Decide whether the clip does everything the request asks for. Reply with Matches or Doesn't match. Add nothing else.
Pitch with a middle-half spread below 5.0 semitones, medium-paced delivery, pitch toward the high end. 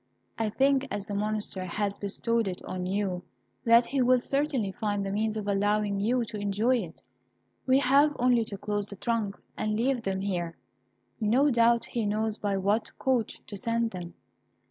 Matches